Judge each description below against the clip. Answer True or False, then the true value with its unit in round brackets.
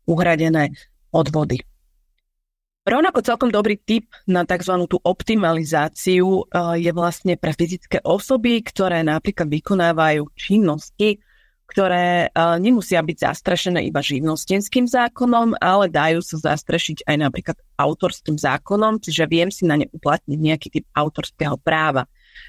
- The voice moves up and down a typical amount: True (4.0 semitones)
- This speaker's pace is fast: False (115 wpm)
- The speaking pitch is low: False (170 Hz)